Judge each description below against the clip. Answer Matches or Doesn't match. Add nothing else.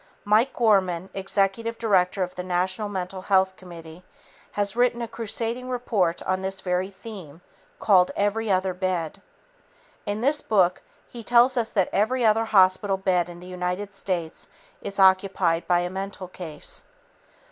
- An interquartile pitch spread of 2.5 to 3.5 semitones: Matches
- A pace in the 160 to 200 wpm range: Doesn't match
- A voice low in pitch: Doesn't match